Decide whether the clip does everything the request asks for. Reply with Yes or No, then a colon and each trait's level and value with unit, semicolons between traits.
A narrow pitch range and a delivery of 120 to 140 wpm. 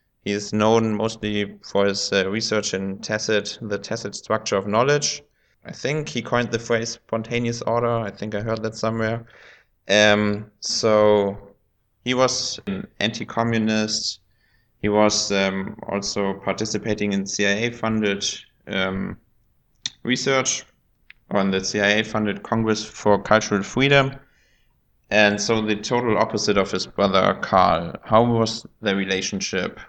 Yes: narrow, 2.1 semitones; slow, 135 wpm